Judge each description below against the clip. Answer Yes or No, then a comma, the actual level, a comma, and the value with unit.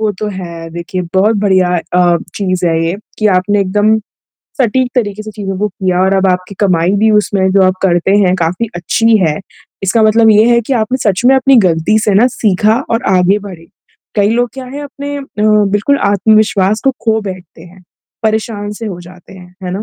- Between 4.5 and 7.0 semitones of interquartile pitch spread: No, average, 3.1 semitones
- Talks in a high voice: Yes, high, 200 Hz